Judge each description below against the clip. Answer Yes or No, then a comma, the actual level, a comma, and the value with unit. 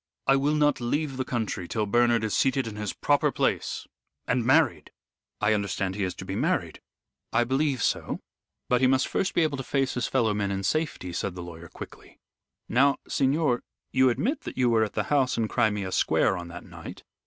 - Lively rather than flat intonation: No, average, 5.0 semitones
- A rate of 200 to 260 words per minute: Yes, fast, 205 wpm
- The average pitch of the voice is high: No, low, 120 Hz